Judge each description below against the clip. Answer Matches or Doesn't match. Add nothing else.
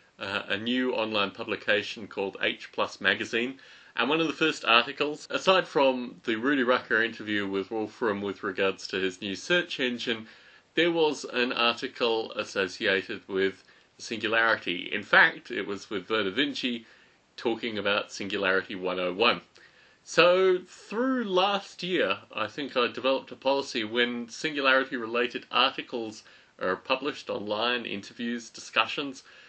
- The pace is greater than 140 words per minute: Doesn't match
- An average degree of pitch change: Matches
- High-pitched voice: Doesn't match